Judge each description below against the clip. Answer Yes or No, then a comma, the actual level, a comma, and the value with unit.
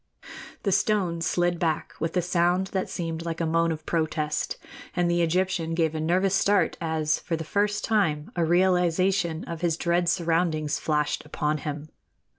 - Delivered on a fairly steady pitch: Yes, narrow, 2.2 semitones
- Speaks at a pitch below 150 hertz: No, medium, 170 Hz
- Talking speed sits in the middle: Yes, average, 170 wpm